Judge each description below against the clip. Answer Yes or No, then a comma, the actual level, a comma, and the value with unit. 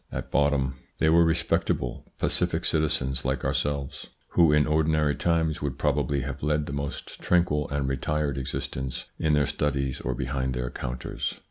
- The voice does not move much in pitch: Yes, narrow, 2.3 semitones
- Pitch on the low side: Yes, very low, 70 Hz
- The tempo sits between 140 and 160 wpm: Yes, average, 155 wpm